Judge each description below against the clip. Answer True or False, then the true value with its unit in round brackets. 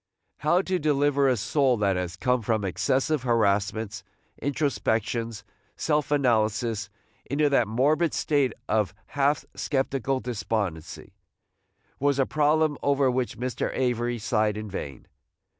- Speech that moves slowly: True (125 wpm)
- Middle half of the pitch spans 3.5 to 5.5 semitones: True (4.7 semitones)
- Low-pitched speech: True (125 Hz)